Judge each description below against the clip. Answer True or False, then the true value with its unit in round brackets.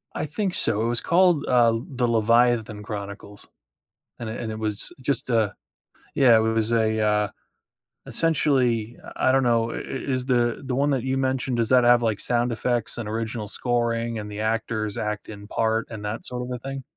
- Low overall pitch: True (115 Hz)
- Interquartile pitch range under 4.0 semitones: True (2.4 semitones)